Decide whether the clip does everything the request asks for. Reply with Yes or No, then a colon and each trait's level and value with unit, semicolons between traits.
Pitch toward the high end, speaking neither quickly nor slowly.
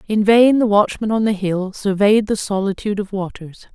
Yes: high, 205 Hz; average, 190 wpm